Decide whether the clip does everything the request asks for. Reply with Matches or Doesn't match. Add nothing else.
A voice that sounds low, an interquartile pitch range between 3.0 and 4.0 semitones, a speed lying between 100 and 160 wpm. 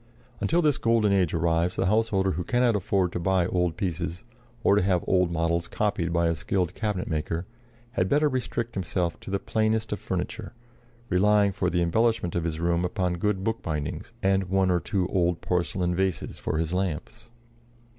Doesn't match